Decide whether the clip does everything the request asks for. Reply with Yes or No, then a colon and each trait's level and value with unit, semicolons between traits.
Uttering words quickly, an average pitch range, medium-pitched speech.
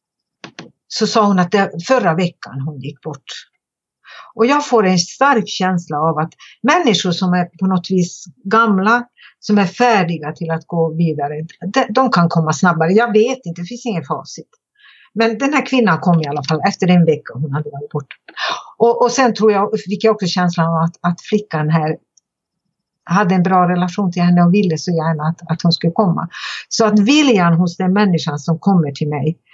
Yes: fast, 200 wpm; average, 4.8 semitones; medium, 180 Hz